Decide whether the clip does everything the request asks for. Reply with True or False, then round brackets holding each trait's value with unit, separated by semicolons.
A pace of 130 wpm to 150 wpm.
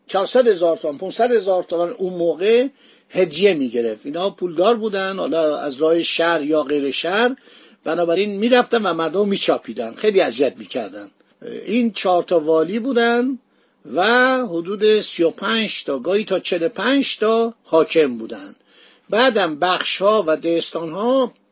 True (140 wpm)